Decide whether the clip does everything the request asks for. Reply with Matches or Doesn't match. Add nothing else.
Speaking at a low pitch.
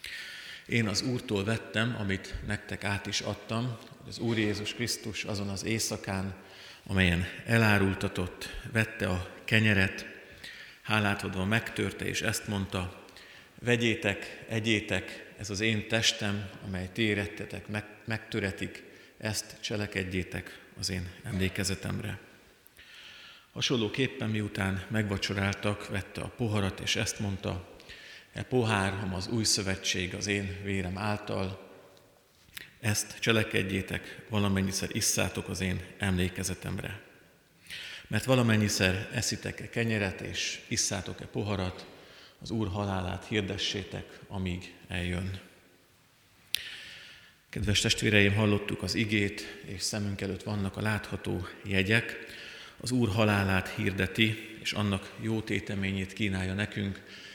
Matches